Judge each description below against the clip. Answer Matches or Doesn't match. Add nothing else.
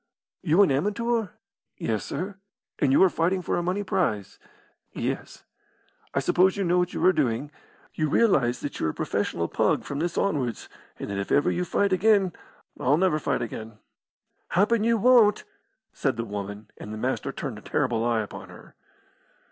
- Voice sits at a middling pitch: Matches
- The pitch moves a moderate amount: Doesn't match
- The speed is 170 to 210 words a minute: Matches